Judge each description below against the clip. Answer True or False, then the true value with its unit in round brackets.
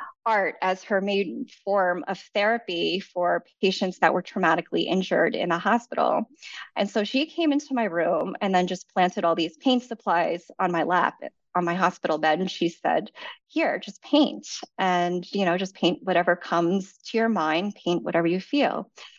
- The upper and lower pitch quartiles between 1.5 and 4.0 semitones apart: False (4.6 semitones)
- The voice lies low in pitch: False (190 Hz)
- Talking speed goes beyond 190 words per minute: False (180 wpm)